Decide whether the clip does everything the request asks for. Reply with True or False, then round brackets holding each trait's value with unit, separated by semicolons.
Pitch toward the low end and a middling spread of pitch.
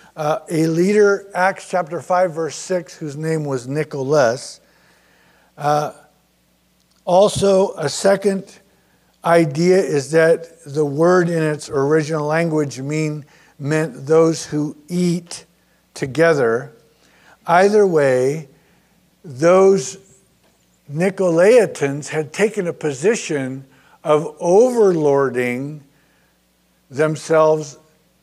False (155 Hz; 3.6 semitones)